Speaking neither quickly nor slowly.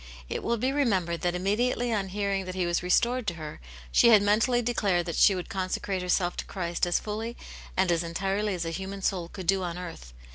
No: fast, 220 wpm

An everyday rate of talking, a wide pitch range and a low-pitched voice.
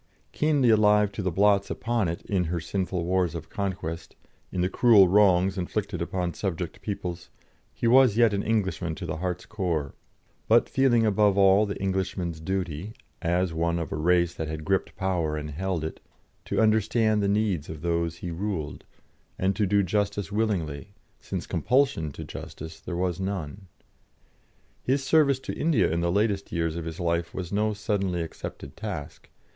No: average, 175 wpm; average, 3.7 semitones; very low, 95 Hz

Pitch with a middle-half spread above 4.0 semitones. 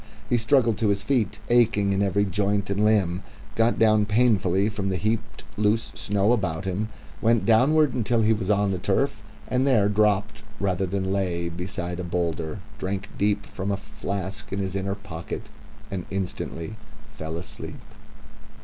No: narrow, 2.4 semitones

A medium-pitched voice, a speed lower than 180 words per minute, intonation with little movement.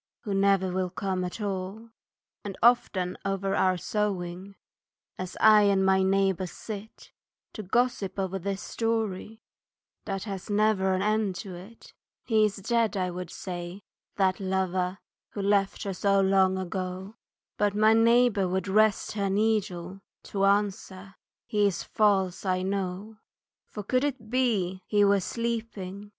No: high, 195 Hz; average, 145 wpm; narrow, 2.2 semitones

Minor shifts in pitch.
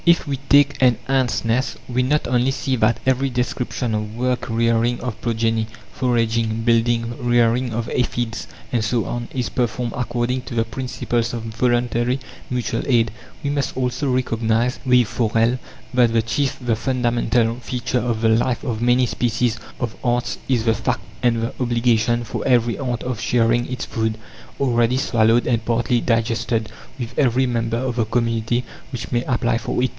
Yes: narrow, 1.6 semitones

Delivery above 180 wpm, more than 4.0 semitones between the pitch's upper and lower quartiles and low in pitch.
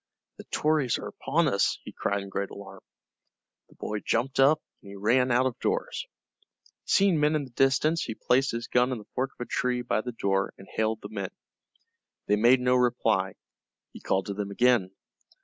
Yes: average, 195 wpm; average, 4.8 semitones; low, 120 Hz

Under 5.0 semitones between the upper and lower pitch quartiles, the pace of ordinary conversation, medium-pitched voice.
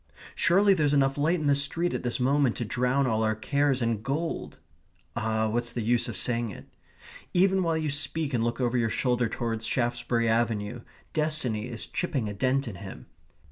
No: average, 3.9 semitones; average, 190 wpm; low, 125 Hz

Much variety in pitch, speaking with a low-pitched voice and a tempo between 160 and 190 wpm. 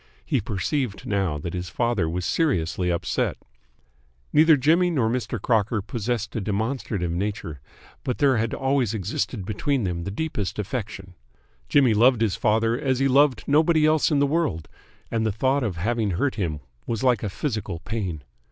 Yes: wide, 5.7 semitones; low, 115 Hz; average, 170 wpm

